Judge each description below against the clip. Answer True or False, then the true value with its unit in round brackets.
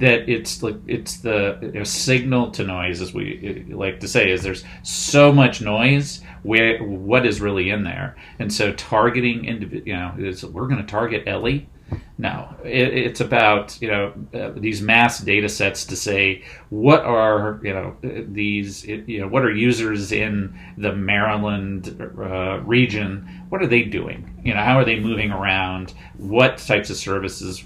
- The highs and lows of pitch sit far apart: False (3.5 semitones)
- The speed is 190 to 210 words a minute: False (175 wpm)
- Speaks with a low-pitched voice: True (105 Hz)